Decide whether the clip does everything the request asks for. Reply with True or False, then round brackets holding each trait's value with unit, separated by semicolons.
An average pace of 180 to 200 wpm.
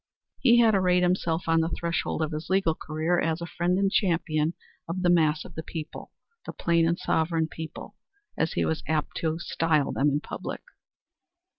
True (185 wpm)